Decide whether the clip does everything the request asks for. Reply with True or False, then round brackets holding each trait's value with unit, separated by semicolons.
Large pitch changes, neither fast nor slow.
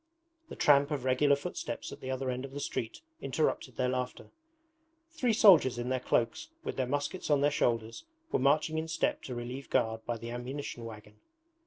False (3.1 semitones; 190 wpm)